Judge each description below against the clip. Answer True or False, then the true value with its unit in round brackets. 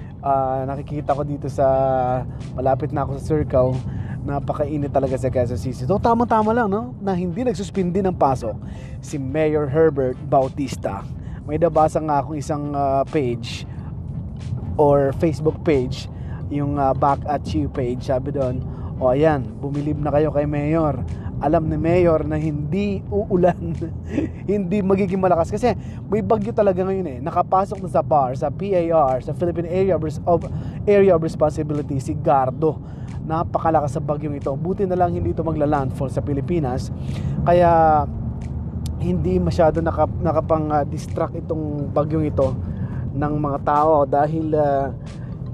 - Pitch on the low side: False (150 Hz)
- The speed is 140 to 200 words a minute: True (150 wpm)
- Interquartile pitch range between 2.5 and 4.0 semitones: True (3.5 semitones)